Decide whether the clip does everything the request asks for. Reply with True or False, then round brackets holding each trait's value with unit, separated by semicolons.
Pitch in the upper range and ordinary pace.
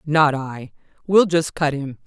False (150 Hz; 145 wpm)